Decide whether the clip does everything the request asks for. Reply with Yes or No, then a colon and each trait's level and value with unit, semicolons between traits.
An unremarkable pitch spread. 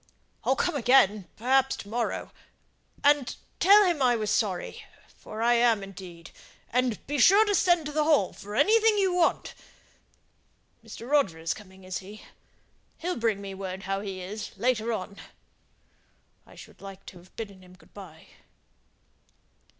No: wide, 6.6 semitones